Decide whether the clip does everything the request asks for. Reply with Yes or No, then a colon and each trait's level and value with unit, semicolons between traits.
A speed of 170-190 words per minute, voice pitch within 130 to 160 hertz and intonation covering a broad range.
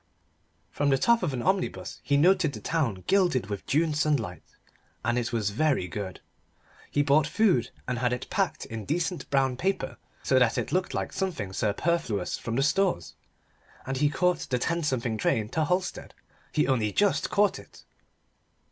Yes: average, 175 wpm; medium, 140 Hz; wide, 6.6 semitones